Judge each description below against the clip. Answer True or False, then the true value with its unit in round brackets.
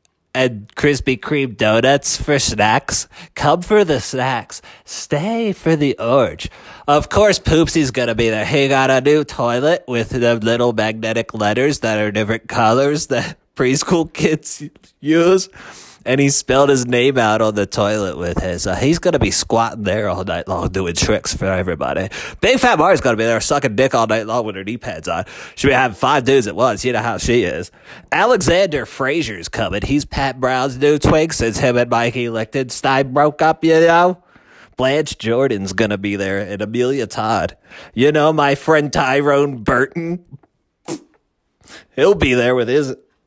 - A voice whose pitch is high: False (130 Hz)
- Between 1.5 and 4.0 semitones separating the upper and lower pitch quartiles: False (4.9 semitones)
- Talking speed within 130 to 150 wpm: False (180 wpm)